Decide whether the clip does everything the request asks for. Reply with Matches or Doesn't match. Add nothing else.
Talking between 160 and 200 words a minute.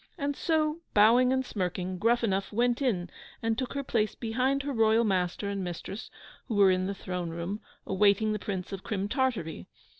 Matches